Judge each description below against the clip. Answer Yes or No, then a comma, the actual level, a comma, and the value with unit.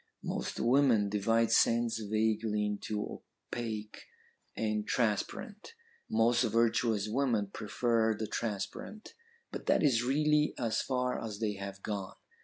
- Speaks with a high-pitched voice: No, low, 115 Hz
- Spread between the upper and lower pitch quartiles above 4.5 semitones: No, narrow, 2.4 semitones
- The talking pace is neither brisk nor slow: No, slow, 120 wpm